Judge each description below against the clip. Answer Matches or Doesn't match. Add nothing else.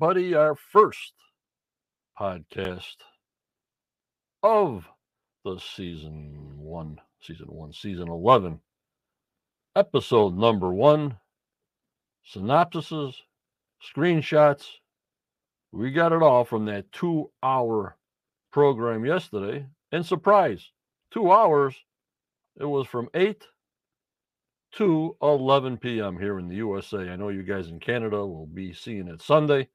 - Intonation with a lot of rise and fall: Matches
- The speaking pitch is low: Matches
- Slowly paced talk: Matches